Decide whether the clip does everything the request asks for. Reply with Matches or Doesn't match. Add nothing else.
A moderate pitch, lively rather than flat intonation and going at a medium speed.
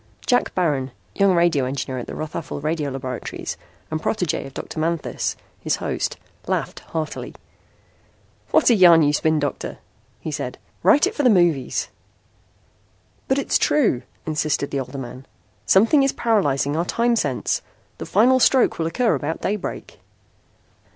Matches